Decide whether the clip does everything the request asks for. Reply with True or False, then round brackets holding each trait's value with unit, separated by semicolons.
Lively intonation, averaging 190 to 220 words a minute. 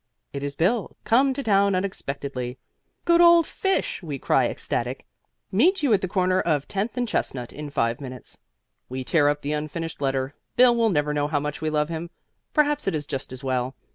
True (7.4 semitones; 200 wpm)